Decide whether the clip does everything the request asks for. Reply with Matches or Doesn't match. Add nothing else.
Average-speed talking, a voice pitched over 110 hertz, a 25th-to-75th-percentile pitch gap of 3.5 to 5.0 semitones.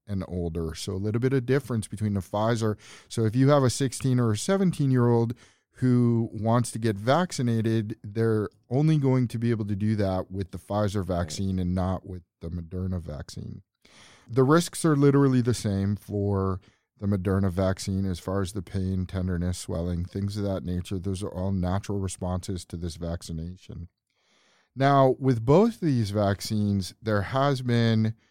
Doesn't match